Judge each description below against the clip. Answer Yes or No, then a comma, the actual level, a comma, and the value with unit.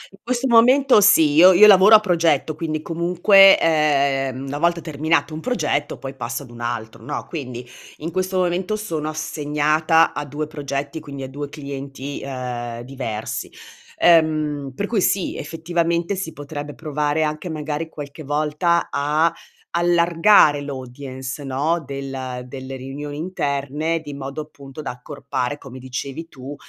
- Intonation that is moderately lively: Yes, average, 3.4 semitones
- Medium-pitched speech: Yes, medium, 150 Hz